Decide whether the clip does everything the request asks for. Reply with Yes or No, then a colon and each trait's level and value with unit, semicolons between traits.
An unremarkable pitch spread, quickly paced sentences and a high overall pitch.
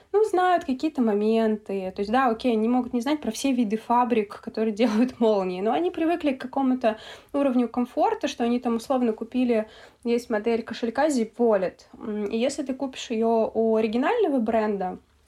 Yes: average, 3.1 semitones; fast, 170 wpm; high, 235 Hz